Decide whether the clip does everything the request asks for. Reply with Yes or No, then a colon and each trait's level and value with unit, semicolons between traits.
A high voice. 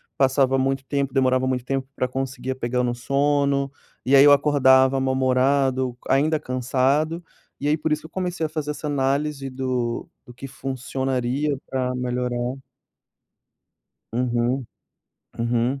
No: low, 135 Hz